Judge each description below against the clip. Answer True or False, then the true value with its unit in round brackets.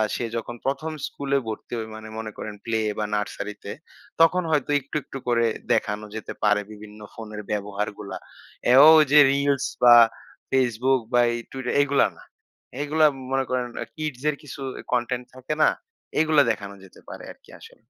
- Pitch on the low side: True (125 Hz)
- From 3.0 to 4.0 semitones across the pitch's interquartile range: False (4.5 semitones)